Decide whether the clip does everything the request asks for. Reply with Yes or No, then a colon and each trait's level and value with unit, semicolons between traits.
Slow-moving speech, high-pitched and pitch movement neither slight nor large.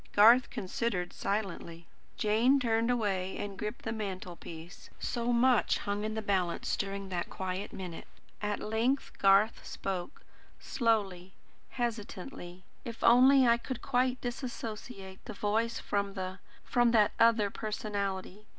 Yes: slow, 130 wpm; high, 210 Hz; average, 3.4 semitones